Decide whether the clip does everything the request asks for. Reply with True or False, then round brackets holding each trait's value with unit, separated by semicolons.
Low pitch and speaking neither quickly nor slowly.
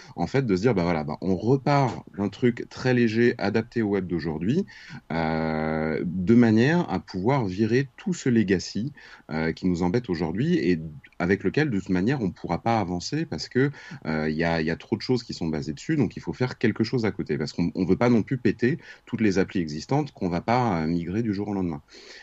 False (95 Hz; 235 wpm)